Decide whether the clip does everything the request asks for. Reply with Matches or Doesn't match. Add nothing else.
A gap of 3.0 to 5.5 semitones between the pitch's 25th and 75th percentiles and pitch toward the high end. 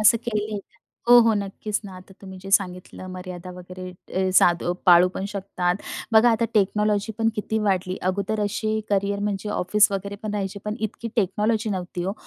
Doesn't match